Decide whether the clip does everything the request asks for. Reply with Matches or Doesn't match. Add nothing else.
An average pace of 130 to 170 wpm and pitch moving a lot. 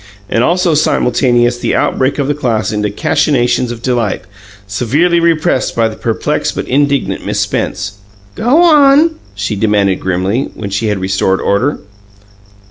Matches